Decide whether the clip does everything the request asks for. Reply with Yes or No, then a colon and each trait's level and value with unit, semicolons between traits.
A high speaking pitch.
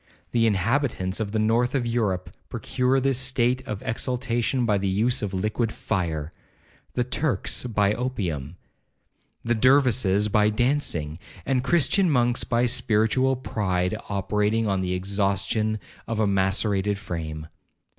No: low, 110 Hz